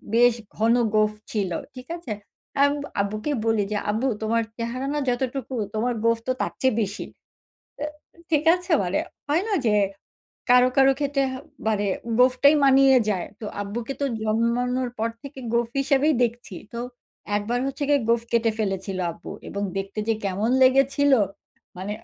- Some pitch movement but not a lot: Yes, average, 4.0 semitones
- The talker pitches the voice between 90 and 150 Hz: No, high, 235 Hz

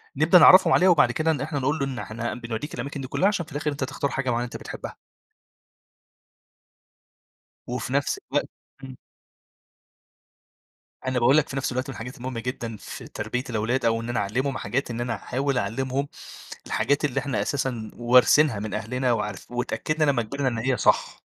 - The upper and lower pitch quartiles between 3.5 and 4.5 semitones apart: No, average, 3.1 semitones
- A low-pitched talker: Yes, low, 130 Hz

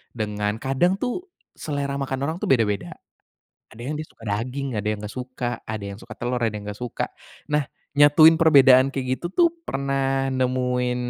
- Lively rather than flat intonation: No, average, 3.4 semitones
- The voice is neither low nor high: No, low, 130 Hz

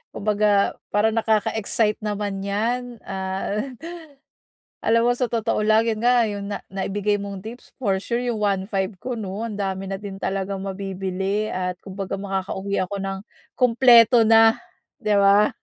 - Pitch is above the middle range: Yes, high, 205 Hz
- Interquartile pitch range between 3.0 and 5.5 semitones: No, narrow, 2.5 semitones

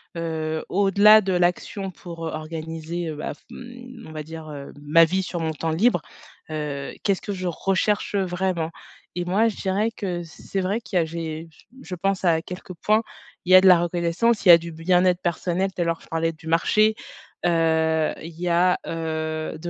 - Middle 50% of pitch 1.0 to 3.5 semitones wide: Yes, average, 2.9 semitones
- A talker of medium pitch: Yes, medium, 175 Hz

